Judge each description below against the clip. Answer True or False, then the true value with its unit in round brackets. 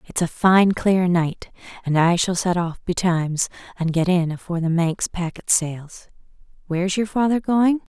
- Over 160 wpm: True (175 wpm)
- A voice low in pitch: False (180 Hz)